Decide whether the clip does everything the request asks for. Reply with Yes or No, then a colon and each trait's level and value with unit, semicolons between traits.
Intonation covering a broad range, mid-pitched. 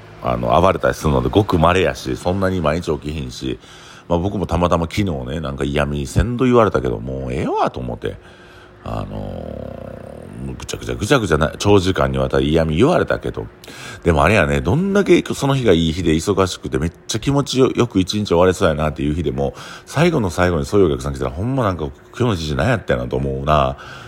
No: wide, 7.2 semitones; very low, 85 Hz